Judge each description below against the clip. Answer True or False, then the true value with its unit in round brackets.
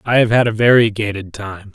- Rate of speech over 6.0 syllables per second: False (5.5 syllables/s)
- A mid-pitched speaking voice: False (110 Hz)